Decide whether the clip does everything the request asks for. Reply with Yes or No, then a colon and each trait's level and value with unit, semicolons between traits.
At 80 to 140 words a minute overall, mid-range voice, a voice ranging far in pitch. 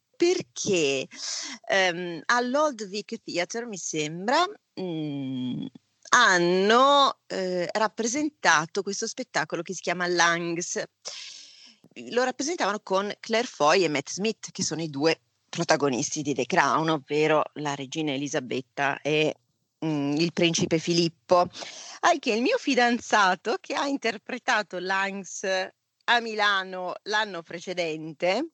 Yes: slow, 115 wpm; medium, 180 Hz; wide, 6.4 semitones